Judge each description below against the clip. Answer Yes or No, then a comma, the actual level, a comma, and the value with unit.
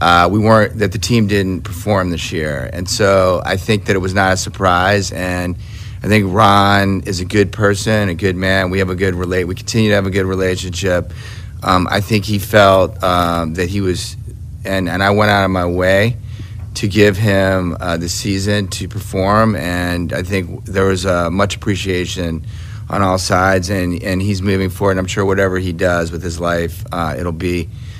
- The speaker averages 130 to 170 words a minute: No, fast, 205 wpm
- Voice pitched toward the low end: Yes, very low, 95 Hz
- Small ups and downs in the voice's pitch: Yes, narrow, 2.2 semitones